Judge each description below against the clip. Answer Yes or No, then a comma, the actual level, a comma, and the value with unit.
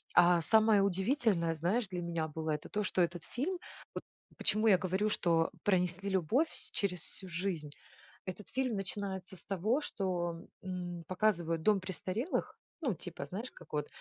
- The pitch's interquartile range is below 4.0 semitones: Yes, average, 3.5 semitones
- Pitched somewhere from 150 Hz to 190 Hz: Yes, medium, 185 Hz